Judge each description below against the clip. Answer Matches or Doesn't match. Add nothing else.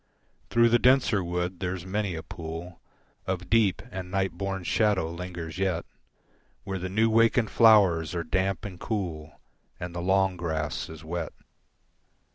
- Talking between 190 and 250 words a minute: Doesn't match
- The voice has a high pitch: Doesn't match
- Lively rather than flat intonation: Doesn't match